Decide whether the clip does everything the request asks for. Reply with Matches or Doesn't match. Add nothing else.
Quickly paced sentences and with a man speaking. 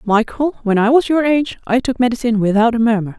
Doesn't match